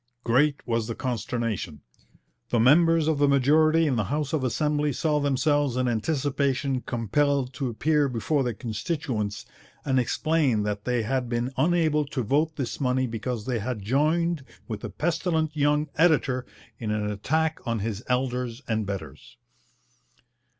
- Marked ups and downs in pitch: No, average, 4.4 semitones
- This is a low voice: Yes, low, 130 Hz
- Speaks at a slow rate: No, average, 150 wpm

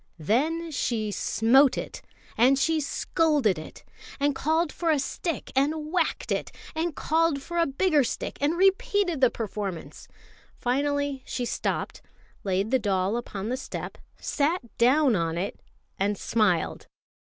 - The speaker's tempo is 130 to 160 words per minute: Yes, average, 145 wpm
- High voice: Yes, very high, 275 Hz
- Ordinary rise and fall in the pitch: No, wide, 6.3 semitones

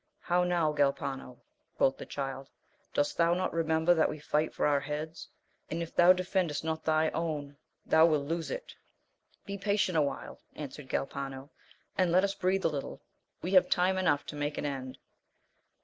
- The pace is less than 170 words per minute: No, average, 175 wpm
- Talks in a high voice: No, medium, 160 Hz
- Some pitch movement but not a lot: Yes, average, 3.6 semitones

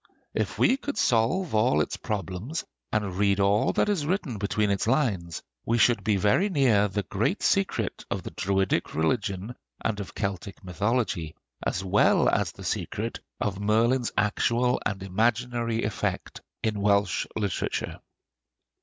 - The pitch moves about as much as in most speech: Yes, average, 3.4 semitones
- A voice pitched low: Yes, low, 105 Hz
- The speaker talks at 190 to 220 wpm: No, average, 145 wpm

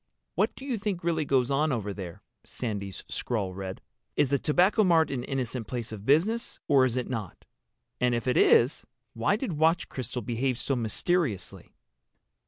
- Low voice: Yes, low, 130 Hz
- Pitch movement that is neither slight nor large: No, wide, 6.0 semitones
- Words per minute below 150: No, average, 170 wpm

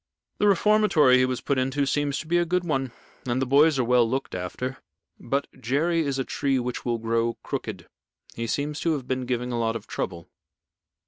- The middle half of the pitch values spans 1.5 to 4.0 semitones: Yes, average, 3.5 semitones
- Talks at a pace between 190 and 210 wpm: Yes, fast, 205 wpm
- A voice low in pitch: Yes, low, 130 Hz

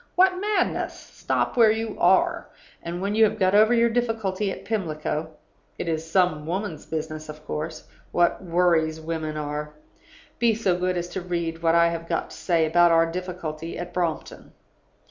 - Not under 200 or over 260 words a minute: No, average, 175 wpm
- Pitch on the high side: No, medium, 175 Hz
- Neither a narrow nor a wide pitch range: Yes, average, 4.1 semitones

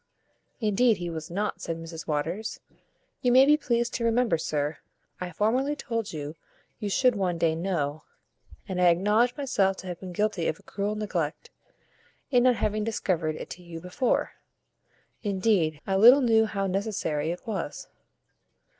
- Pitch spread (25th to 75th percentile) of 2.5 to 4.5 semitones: No, average, 5.3 semitones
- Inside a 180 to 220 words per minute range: No, average, 165 wpm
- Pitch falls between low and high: No, high, 195 Hz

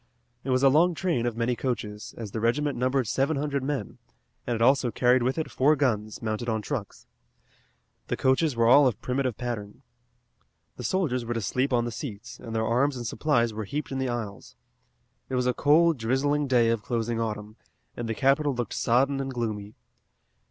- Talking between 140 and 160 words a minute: No, average, 195 wpm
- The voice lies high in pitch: No, low, 125 Hz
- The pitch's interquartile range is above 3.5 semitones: No, average, 3.2 semitones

